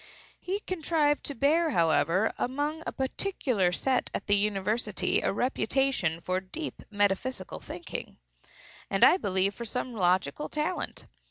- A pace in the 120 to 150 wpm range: Yes, slow, 135 wpm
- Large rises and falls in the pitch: Yes, wide, 7.3 semitones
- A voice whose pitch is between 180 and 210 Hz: No, high, 240 Hz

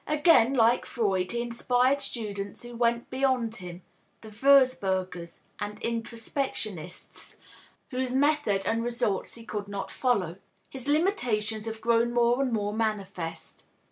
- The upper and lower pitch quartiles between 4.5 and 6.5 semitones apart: No, average, 3.6 semitones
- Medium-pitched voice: No, high, 230 Hz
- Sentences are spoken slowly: Yes, slow, 130 wpm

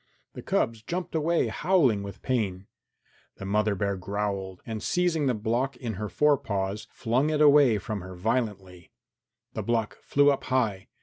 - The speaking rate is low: No, average, 165 wpm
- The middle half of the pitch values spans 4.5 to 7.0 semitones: Yes, wide, 5.5 semitones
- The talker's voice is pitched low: Yes, low, 110 Hz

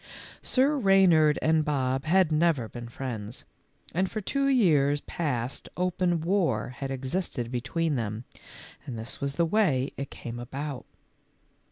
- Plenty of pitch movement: Yes, wide, 5.7 semitones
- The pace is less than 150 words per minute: Yes, average, 140 wpm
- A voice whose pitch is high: No, medium, 145 Hz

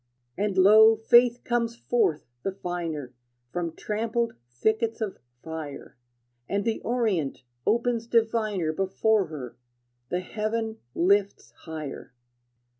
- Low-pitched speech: No, high, 205 Hz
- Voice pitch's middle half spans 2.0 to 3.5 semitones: No, average, 5.2 semitones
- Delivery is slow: Yes, slow, 110 wpm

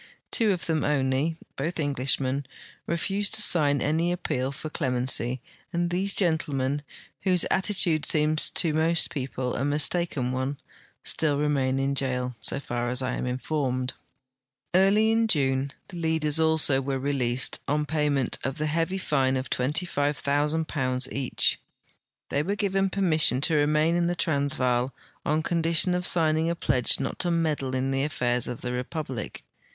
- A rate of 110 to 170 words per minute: Yes, average, 155 wpm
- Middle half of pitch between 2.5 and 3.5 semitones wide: No, average, 4.0 semitones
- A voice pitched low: No, medium, 150 Hz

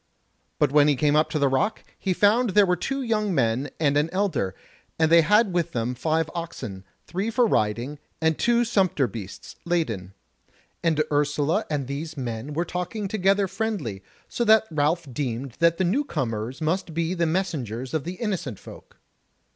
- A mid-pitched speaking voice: Yes, medium, 160 Hz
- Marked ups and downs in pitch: Yes, wide, 5.9 semitones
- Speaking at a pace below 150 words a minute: No, average, 175 wpm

